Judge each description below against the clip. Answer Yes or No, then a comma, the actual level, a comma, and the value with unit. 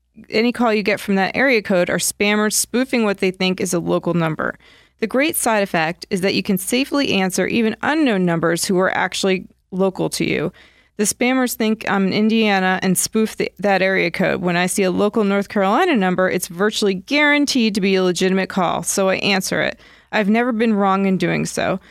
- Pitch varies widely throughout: No, average, 3.1 semitones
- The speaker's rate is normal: No, fast, 210 wpm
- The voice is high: Yes, high, 200 Hz